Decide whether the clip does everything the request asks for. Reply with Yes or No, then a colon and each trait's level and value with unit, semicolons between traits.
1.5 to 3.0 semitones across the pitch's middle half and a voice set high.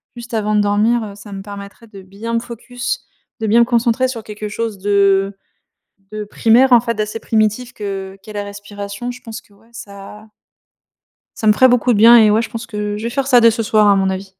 Yes: narrow, 2.4 semitones; high, 215 Hz